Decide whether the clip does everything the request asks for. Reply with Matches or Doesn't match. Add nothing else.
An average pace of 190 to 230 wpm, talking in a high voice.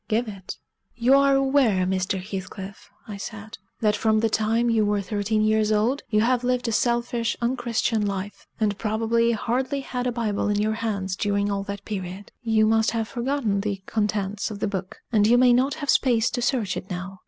Matches